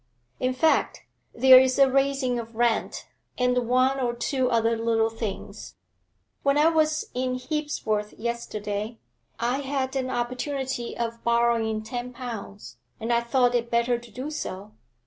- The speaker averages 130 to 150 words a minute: Yes, average, 145 wpm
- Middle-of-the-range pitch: No, high, 245 Hz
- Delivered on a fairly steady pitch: Yes, narrow, 2.1 semitones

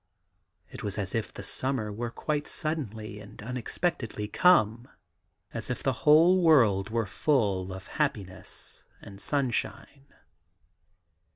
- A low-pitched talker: Yes, low, 115 Hz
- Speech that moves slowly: Yes, slow, 120 wpm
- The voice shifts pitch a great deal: Yes, wide, 5.8 semitones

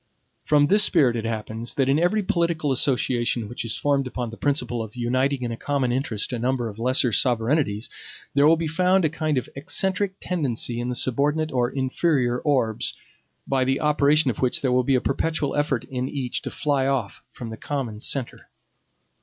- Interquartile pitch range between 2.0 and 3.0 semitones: No, average, 3.5 semitones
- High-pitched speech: No, low, 130 Hz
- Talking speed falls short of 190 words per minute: No, average, 195 wpm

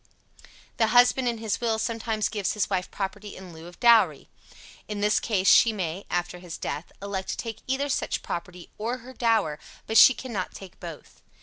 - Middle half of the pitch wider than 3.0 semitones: Yes, average, 4.1 semitones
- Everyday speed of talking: Yes, average, 190 wpm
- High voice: Yes, high, 210 Hz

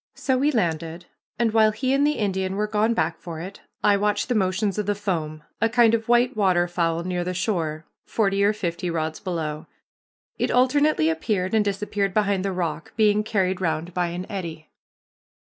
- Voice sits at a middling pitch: No, high, 195 Hz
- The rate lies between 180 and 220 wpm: Yes, average, 185 wpm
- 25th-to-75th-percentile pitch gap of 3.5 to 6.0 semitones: Yes, average, 3.9 semitones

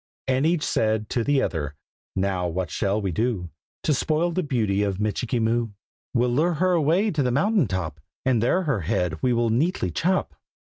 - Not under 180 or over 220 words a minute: Yes, average, 190 wpm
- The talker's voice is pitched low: Yes, low, 120 Hz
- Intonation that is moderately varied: No, wide, 7.6 semitones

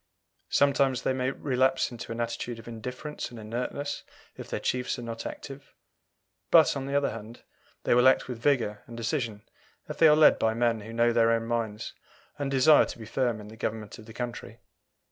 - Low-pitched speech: Yes, low, 120 Hz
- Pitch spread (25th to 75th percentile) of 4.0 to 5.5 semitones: No, narrow, 2.6 semitones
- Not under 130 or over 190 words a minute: No, average, 200 wpm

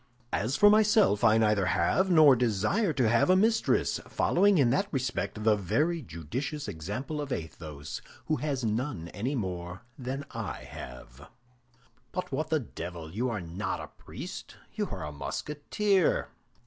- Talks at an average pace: Yes, average, 155 wpm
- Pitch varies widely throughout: Yes, wide, 8.8 semitones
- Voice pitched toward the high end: No, low, 125 Hz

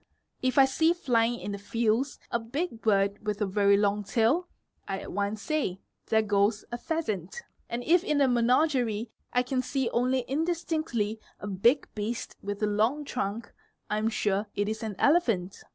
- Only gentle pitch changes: No, average, 4.5 semitones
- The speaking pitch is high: Yes, high, 230 Hz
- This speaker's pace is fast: No, average, 175 wpm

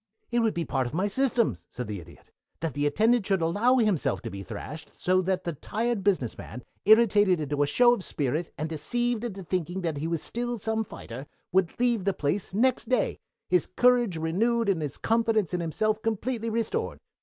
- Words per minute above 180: Yes, average, 200 wpm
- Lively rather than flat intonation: Yes, wide, 6.2 semitones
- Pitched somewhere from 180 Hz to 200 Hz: Yes, high, 190 Hz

